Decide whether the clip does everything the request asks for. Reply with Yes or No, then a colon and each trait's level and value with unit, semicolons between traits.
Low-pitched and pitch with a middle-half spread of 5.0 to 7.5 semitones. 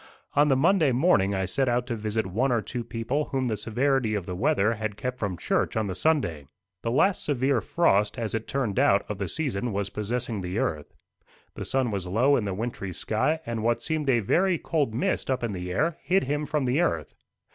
Yes: low, 120 Hz; average, 5.3 semitones